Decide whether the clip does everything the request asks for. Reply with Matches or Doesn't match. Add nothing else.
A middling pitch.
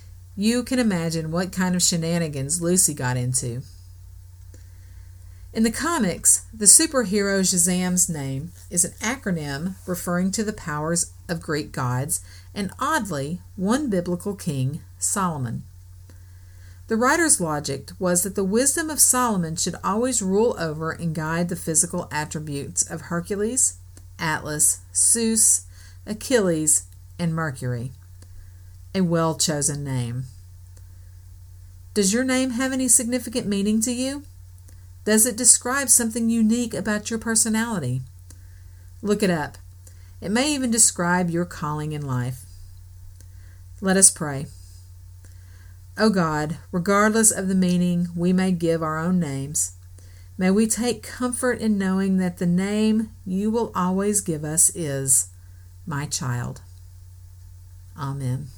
Matches